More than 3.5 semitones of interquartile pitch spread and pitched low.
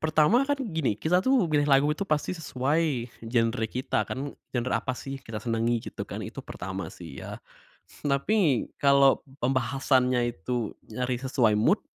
Yes: average, 4.1 semitones; low, 130 Hz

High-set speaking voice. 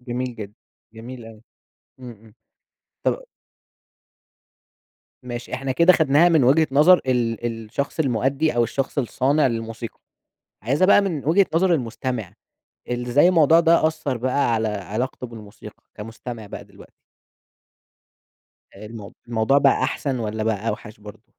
No: low, 125 Hz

